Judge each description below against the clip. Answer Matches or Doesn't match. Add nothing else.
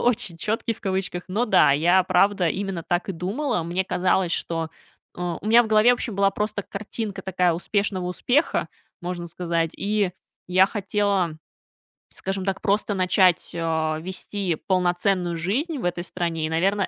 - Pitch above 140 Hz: Matches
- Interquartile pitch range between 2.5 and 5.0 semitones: Matches